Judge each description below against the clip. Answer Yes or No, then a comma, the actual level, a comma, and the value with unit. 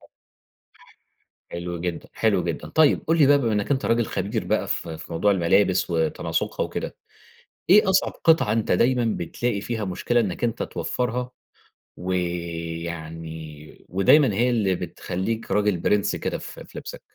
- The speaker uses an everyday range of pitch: No, wide, 5.8 semitones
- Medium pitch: No, low, 100 Hz